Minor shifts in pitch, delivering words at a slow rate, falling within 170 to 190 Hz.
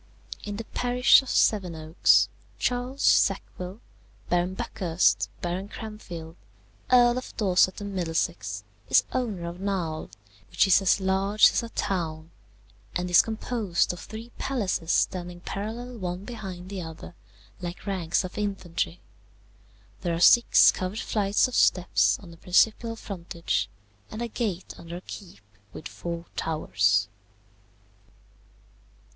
No: average, 3.9 semitones; slow, 130 wpm; medium, 185 Hz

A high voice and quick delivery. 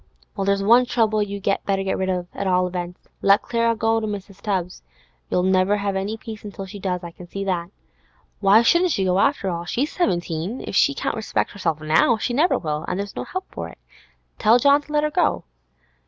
Yes: high, 200 Hz; fast, 220 wpm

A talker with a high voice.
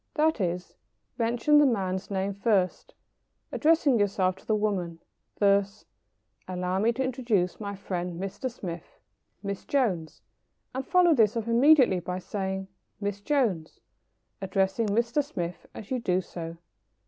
Yes: high, 200 Hz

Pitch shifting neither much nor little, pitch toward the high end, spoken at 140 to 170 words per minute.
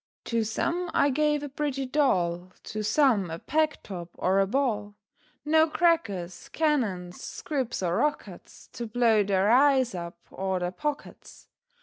No: wide, 7.6 semitones; high, 230 Hz; average, 145 wpm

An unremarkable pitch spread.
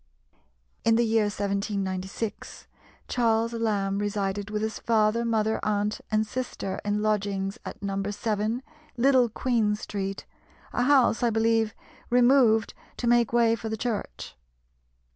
No: narrow, 2.2 semitones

